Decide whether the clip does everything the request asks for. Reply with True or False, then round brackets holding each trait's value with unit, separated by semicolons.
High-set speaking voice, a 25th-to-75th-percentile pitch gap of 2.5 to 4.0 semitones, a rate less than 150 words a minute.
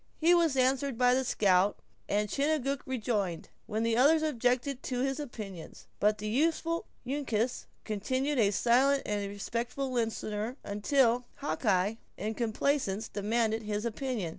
False (240 Hz; 4.4 semitones; 140 wpm)